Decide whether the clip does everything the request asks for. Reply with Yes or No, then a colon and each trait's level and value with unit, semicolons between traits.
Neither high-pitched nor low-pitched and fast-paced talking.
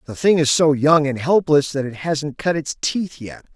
Yes: medium, 150 Hz; fast, 235 wpm